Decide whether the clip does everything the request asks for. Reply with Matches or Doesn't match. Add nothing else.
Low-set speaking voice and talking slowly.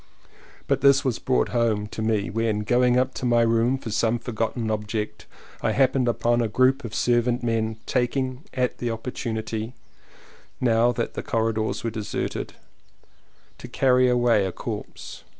Doesn't match